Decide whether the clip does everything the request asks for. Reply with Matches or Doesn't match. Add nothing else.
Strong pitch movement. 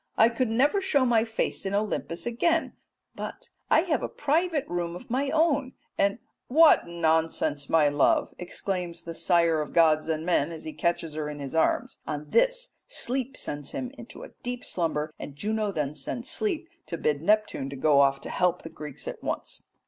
Matches